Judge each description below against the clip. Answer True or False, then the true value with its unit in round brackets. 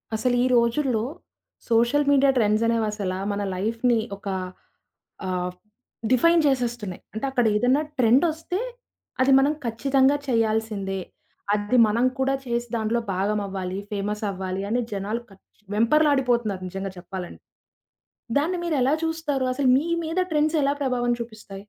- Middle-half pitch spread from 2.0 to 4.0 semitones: False (4.6 semitones)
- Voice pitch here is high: True (235 Hz)